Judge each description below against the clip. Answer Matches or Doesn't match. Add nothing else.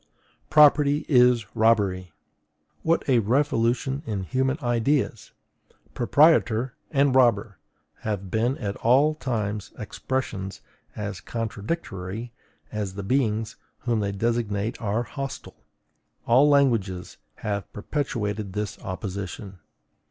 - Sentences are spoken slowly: Matches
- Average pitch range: Matches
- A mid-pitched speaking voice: Doesn't match